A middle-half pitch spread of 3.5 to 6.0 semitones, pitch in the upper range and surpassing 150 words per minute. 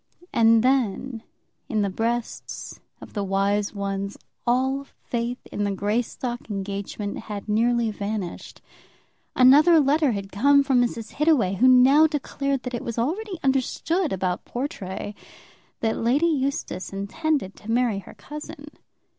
No: average, 5.1 semitones; high, 235 Hz; slow, 135 wpm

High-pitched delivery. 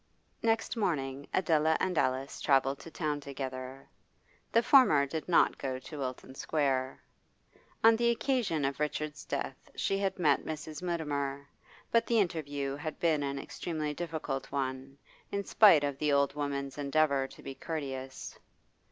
No: medium, 145 Hz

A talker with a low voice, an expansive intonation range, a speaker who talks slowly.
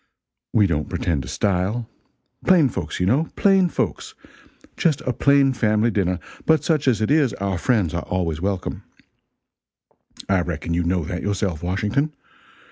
No: low, 100 Hz; wide, 7.1 semitones; average, 155 wpm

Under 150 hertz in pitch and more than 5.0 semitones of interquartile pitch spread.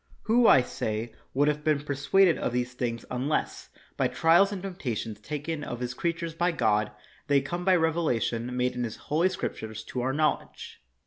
Yes: medium, 140 Hz; wide, 5.5 semitones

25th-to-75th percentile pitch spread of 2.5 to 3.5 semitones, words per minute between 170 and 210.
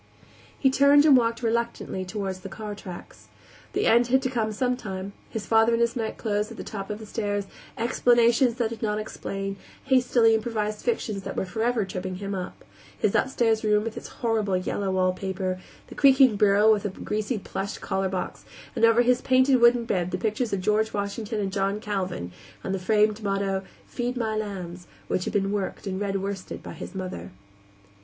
Yes: average, 3.1 semitones; average, 185 wpm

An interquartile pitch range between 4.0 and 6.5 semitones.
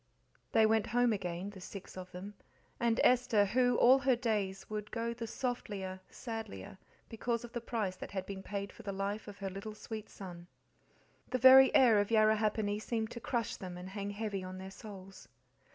No: average, 3.2 semitones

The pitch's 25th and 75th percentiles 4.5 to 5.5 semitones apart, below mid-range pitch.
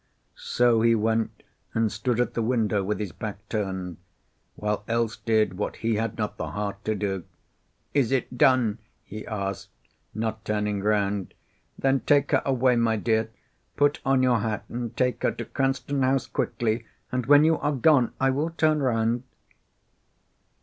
No: average, 3.5 semitones; low, 115 Hz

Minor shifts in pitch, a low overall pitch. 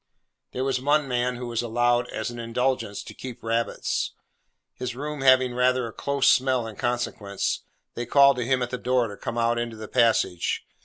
Yes: narrow, 1.7 semitones; low, 120 Hz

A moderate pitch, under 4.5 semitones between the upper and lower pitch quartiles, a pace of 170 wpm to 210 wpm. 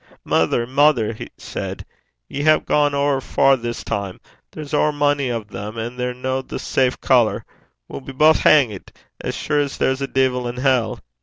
No: low, 130 Hz; average, 3.3 semitones; average, 175 wpm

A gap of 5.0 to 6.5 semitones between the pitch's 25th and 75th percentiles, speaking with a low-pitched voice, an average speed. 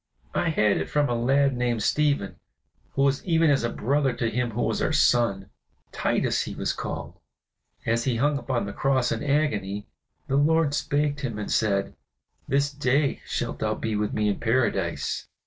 No: average, 4.3 semitones; low, 130 Hz; average, 185 wpm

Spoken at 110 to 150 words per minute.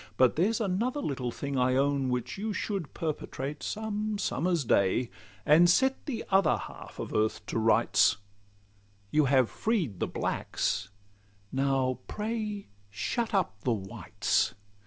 Yes: slow, 135 wpm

